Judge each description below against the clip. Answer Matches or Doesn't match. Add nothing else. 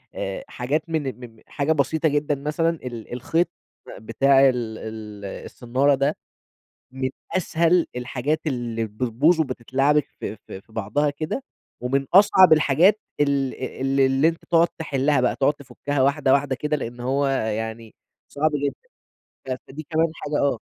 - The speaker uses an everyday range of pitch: Matches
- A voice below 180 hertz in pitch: Matches